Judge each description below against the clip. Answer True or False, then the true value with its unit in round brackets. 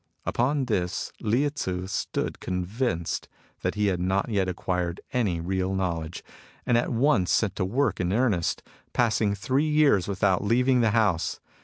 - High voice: False (100 Hz)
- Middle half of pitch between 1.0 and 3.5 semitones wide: False (4.9 semitones)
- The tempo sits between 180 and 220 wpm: False (155 wpm)